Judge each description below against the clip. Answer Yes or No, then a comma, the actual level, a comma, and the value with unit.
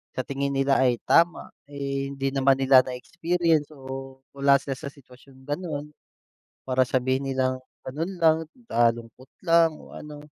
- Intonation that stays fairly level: Yes, narrow, 2.1 semitones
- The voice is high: No, low, 135 Hz